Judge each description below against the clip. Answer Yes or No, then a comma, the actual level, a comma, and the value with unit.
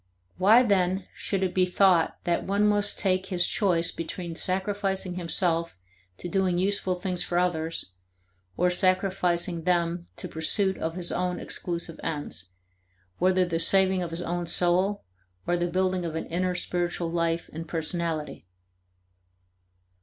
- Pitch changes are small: Yes, narrow, 1.9 semitones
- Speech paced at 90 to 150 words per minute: Yes, average, 145 wpm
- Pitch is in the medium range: Yes, medium, 180 Hz